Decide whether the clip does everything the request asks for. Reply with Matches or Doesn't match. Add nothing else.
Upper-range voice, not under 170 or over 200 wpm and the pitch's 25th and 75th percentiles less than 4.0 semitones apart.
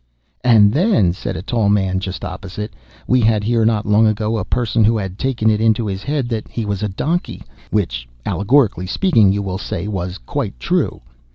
Doesn't match